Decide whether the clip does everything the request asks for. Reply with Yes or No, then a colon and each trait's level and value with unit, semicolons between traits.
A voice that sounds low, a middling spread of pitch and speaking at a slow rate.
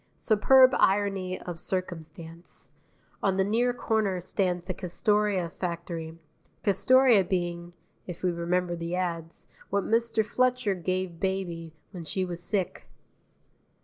No: medium, 185 Hz; average, 3.1 semitones; slow, 120 wpm